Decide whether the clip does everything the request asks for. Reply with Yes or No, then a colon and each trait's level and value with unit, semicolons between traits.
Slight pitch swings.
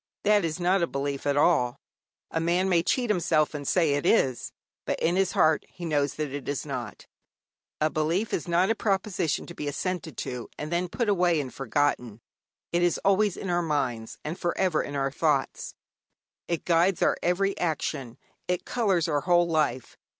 No: average, 3.9 semitones